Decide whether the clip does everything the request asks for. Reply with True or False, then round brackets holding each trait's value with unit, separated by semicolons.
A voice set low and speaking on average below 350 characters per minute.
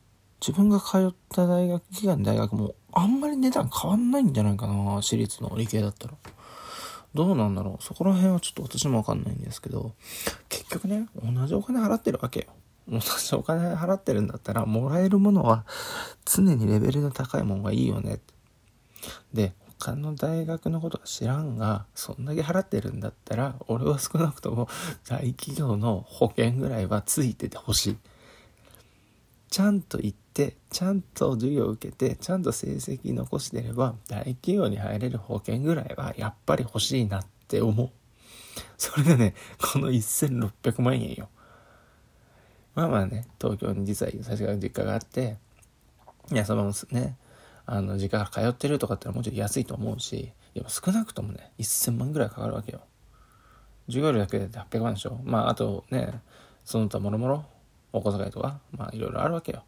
True (120 Hz; 340 characters per minute)